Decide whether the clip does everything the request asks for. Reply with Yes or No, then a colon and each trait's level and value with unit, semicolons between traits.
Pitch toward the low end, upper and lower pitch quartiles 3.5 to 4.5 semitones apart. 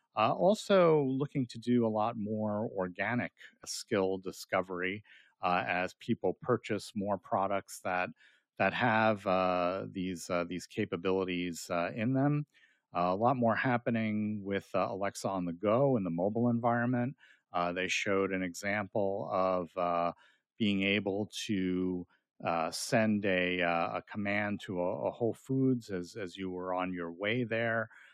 Yes: low, 100 Hz; average, 3.9 semitones